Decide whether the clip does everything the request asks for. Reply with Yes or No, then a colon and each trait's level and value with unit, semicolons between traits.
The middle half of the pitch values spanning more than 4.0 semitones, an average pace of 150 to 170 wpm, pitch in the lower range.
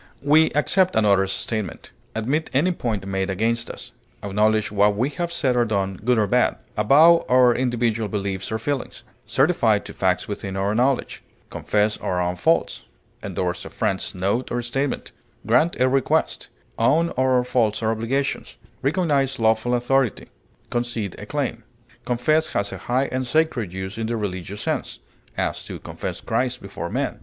Yes: average, 4.4 semitones; average, 160 wpm; low, 115 Hz